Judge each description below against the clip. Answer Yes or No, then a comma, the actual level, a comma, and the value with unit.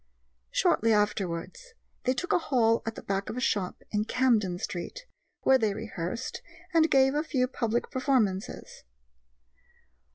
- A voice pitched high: Yes, high, 230 Hz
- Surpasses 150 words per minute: No, average, 140 wpm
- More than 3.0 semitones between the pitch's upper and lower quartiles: Yes, average, 4.4 semitones